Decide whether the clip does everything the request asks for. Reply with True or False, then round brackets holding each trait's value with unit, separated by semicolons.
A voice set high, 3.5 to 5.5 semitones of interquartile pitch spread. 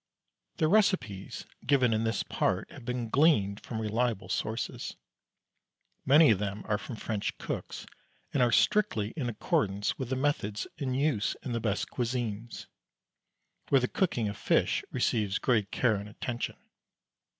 False (115 Hz; 3.8 semitones)